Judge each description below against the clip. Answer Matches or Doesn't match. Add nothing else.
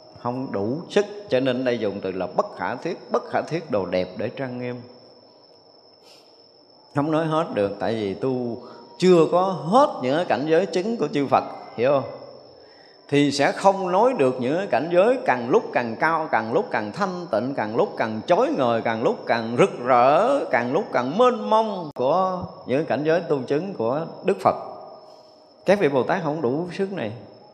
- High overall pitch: Doesn't match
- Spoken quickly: Doesn't match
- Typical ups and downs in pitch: Doesn't match